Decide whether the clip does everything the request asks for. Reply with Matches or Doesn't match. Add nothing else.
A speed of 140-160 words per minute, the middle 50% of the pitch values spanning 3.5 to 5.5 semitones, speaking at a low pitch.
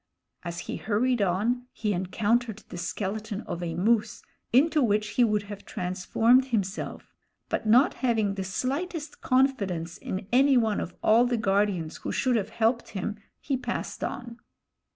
Doesn't match